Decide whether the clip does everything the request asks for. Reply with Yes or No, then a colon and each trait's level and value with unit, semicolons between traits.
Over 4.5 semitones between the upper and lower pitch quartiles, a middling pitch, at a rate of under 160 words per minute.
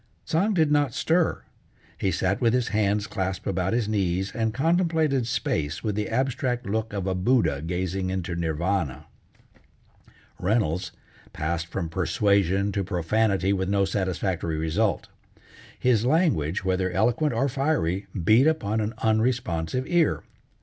No: average, 5.1 semitones; low, 100 Hz; slow, 135 wpm